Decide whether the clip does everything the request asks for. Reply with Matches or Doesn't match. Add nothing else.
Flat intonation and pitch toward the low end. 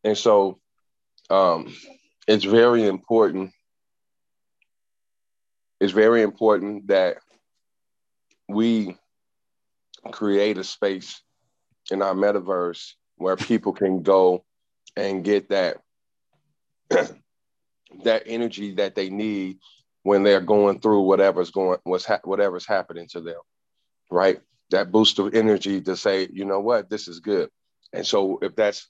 Matches